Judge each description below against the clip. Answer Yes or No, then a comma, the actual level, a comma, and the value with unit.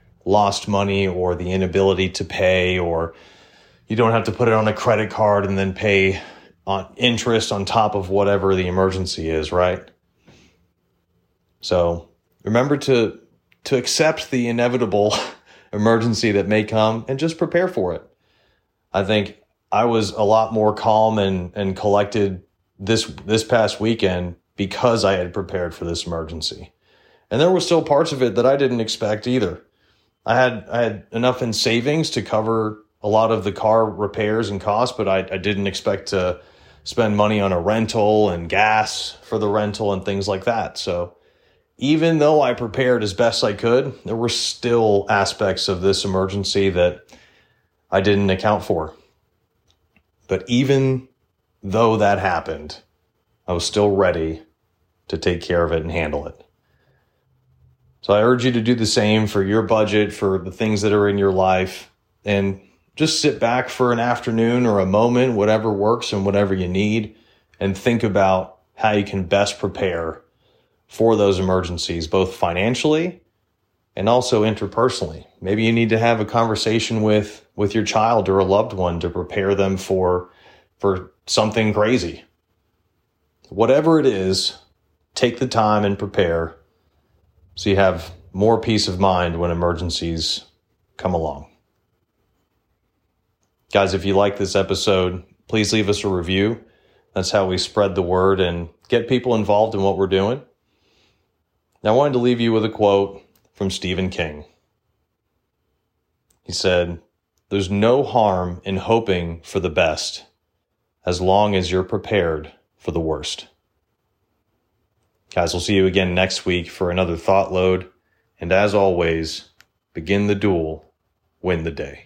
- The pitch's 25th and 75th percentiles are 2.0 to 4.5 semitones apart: Yes, average, 3.1 semitones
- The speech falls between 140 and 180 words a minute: Yes, average, 160 wpm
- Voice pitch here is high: No, low, 100 Hz